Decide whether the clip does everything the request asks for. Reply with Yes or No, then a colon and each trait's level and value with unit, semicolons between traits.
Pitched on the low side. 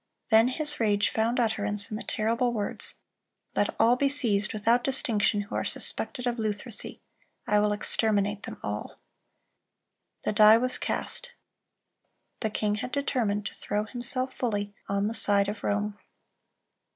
No: high, 215 Hz